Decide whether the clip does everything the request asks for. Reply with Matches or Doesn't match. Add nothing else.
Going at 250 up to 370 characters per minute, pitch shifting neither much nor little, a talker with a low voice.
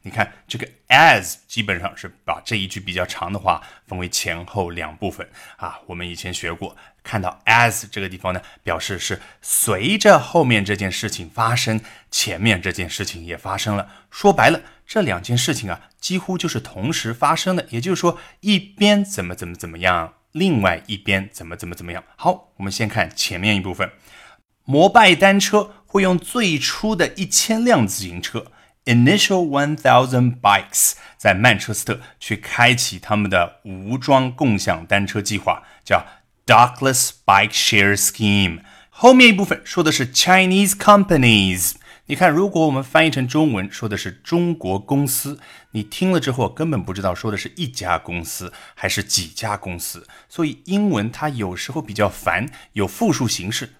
Doesn't match